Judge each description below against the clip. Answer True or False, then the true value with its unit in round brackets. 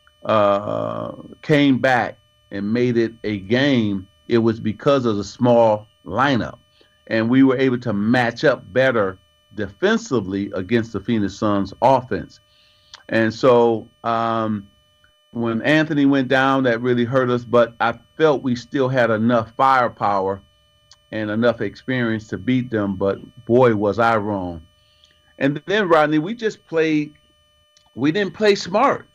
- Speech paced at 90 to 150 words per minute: True (140 wpm)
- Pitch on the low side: True (115 Hz)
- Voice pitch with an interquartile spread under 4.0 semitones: False (4.6 semitones)